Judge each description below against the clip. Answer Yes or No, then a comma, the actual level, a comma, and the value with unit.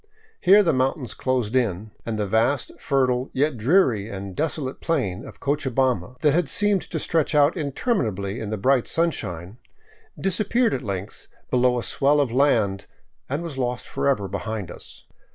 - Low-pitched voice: Yes, low, 130 Hz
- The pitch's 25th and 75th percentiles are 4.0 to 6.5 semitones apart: Yes, wide, 5.6 semitones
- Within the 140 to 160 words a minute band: No, average, 170 wpm